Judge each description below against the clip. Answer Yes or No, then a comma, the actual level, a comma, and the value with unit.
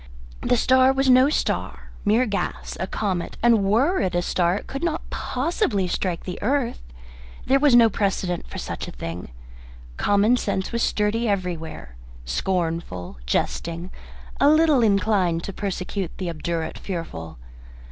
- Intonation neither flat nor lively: No, wide, 5.8 semitones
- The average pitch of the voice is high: Yes, high, 200 Hz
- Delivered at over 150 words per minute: No, average, 145 wpm